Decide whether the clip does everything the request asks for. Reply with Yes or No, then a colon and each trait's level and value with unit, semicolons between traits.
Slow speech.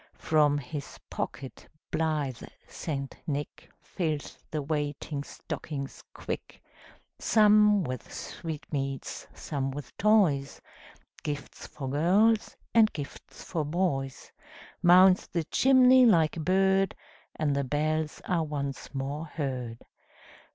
Yes: slow, 110 wpm